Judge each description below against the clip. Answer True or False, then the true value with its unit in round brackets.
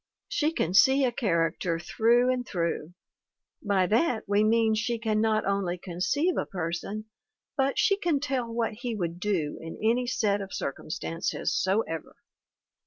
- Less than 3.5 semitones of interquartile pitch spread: False (5.2 semitones)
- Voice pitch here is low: False (215 Hz)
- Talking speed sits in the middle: True (160 wpm)